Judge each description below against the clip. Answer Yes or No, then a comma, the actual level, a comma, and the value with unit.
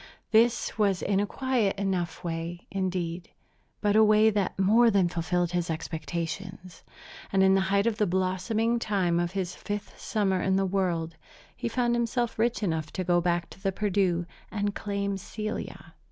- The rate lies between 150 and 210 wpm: Yes, average, 170 wpm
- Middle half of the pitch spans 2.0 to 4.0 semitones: Yes, average, 3.2 semitones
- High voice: Yes, high, 195 Hz